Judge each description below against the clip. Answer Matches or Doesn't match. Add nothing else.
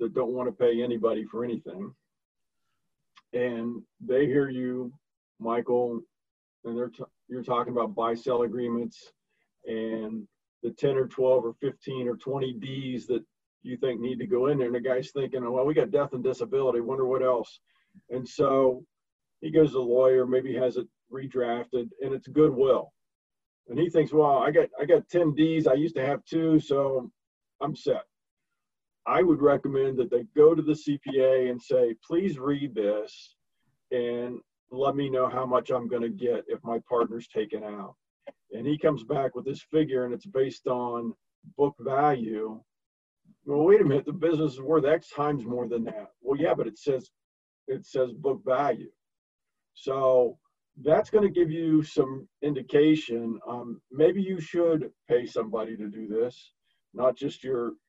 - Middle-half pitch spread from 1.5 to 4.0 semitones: Matches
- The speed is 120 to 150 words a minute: Doesn't match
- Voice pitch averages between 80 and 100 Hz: Doesn't match